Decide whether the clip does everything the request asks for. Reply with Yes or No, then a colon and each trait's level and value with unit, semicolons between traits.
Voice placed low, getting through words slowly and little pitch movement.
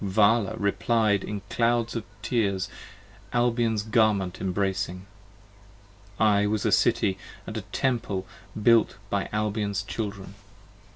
Yes: low, 105 Hz; slow, 115 wpm; narrow, 2.3 semitones